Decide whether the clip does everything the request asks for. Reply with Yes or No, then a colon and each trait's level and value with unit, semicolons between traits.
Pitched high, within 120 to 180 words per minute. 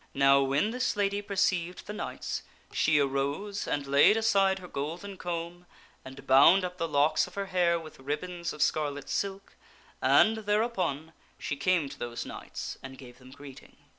No: medium, 170 Hz; average, 165 wpm